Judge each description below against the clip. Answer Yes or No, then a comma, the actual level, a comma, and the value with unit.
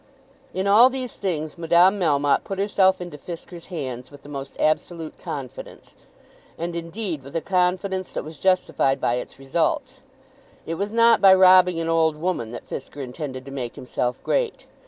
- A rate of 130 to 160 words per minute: No, average, 170 wpm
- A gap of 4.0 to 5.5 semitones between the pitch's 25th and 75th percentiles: Yes, average, 4.8 semitones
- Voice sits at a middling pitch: Yes, medium, 170 Hz